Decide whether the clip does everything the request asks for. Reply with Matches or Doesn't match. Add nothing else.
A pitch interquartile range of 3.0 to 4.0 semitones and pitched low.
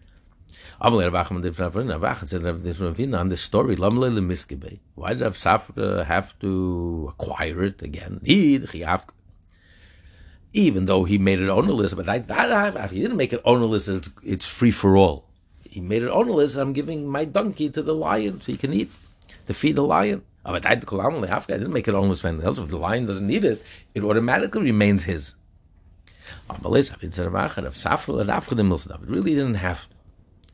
Matches